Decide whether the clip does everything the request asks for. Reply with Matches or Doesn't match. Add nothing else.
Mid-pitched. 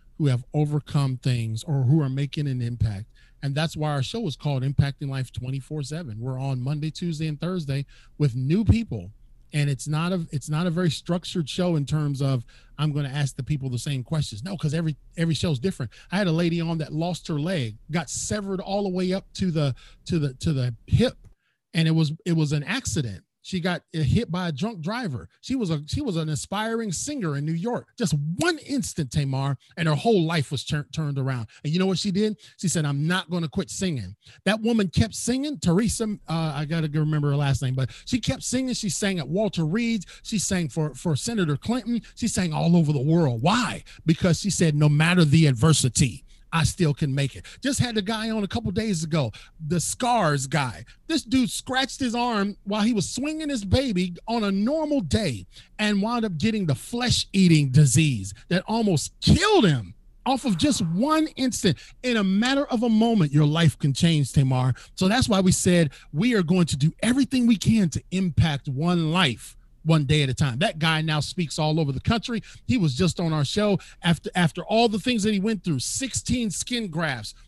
Matches